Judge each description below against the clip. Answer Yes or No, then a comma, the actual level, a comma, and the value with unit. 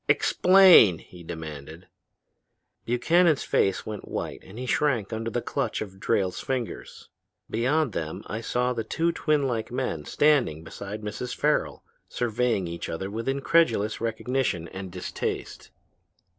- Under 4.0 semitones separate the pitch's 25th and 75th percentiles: No, wide, 5.6 semitones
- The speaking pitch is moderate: No, low, 115 Hz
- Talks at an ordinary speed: No, slow, 130 wpm